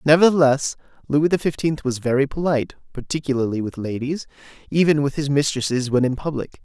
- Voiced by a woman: No, male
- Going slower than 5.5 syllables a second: No, 5.9 syllables/s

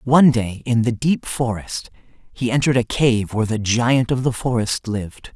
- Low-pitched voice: Yes, low, 120 Hz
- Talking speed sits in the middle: Yes, average, 190 wpm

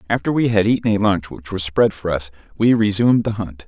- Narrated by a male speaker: Yes, male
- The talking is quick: Yes, fast, 245 wpm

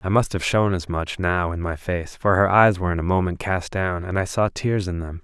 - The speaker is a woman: No, male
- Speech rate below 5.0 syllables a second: No, 5.3 syllables/s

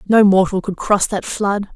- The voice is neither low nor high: No, high, 200 Hz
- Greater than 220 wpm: No, fast, 205 wpm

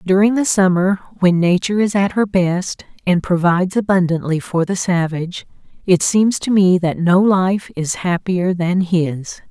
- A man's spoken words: No, female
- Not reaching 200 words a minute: Yes, average, 165 wpm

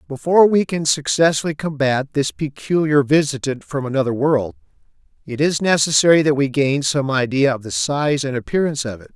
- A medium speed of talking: Yes, average, 170 wpm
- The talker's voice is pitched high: No, medium, 140 Hz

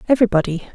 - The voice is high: Yes, high, 205 Hz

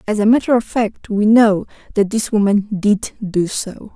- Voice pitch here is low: No, high, 210 Hz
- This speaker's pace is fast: No, average, 195 wpm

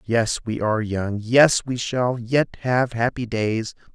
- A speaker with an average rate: Yes, average, 165 wpm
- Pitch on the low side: Yes, low, 115 Hz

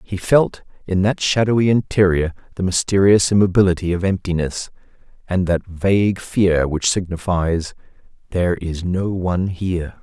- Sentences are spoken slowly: Yes, slow, 125 wpm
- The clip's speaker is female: No, male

